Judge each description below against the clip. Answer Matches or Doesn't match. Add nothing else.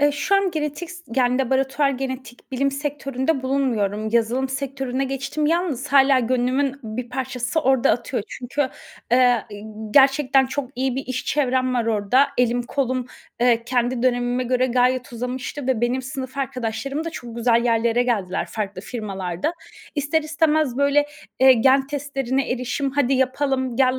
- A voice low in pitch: Doesn't match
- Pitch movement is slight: Matches